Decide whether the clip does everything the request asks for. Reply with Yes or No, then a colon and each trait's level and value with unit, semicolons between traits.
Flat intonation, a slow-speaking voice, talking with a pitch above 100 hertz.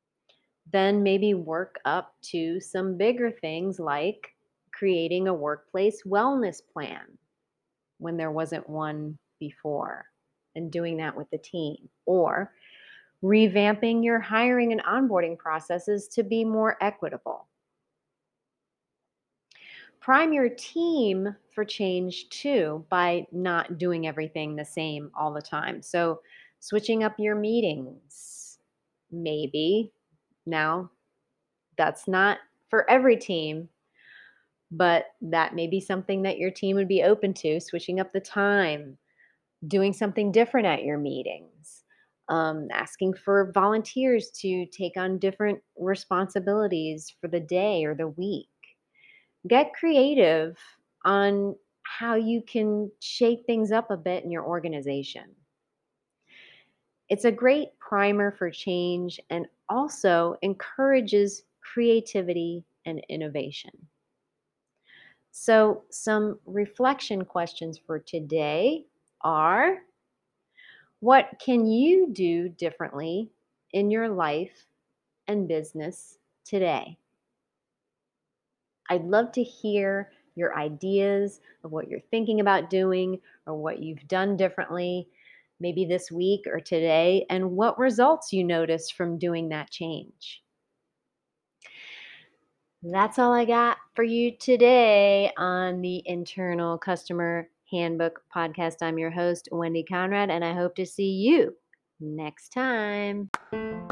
No: average, 4.4 semitones; slow, 115 wpm; medium, 185 Hz